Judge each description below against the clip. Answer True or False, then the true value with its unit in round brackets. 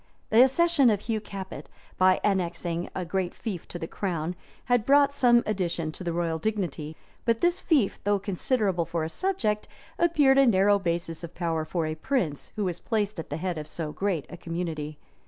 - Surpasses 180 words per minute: True (190 wpm)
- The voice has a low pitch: False (190 Hz)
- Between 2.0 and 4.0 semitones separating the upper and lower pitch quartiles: False (5.2 semitones)